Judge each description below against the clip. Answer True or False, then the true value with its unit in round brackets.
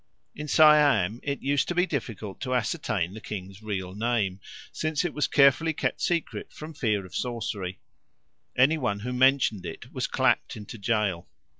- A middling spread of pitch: False (6.1 semitones)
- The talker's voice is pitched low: True (120 Hz)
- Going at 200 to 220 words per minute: False (165 wpm)